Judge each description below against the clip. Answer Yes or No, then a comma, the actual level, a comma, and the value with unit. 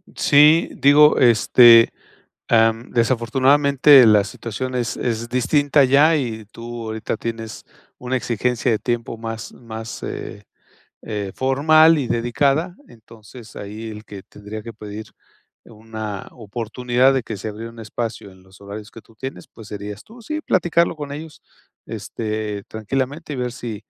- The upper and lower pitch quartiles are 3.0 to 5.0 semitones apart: Yes, average, 3.5 semitones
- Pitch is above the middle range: No, low, 115 Hz